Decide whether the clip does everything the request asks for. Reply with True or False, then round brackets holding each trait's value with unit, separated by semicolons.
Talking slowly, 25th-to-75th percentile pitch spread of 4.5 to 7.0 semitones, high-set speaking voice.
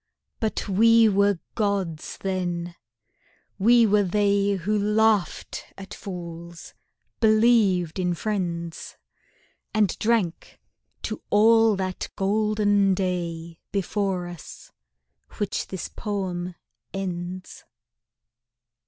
False (90 wpm; 3.0 semitones; 195 Hz)